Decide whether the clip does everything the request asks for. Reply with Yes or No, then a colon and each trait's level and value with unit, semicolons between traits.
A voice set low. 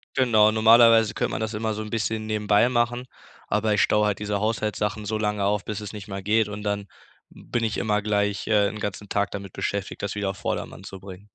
Yes: low, 105 Hz